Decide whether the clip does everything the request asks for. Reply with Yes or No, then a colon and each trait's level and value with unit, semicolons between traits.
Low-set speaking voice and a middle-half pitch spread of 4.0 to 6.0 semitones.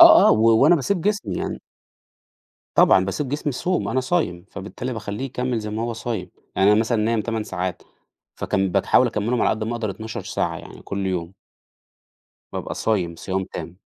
Yes: low, 110 Hz; average, 4.4 semitones